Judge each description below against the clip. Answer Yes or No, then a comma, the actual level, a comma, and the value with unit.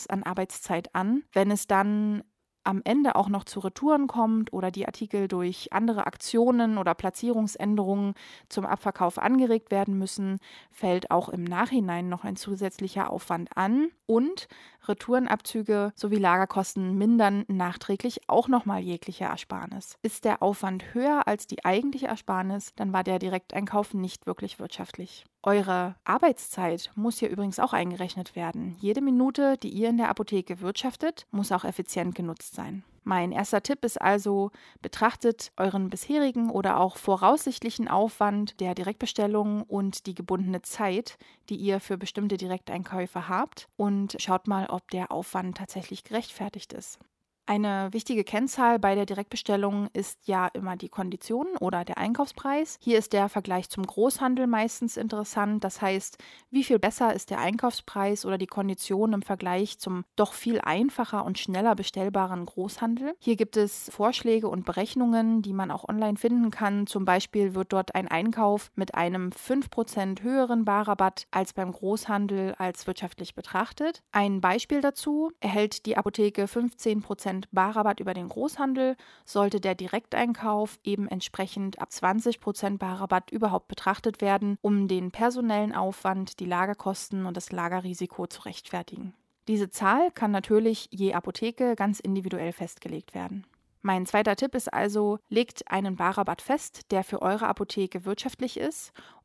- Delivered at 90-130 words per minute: No, average, 150 wpm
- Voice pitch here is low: No, high, 200 Hz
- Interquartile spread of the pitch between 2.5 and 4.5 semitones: Yes, average, 3.0 semitones